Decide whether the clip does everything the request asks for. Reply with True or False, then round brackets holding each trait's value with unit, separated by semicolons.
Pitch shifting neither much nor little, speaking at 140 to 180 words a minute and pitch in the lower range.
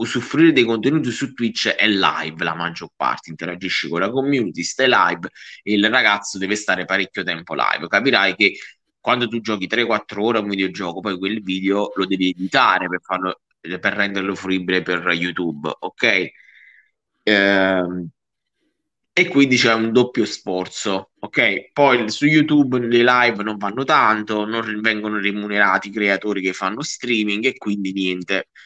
True (3.6 semitones; 155 wpm; 100 Hz)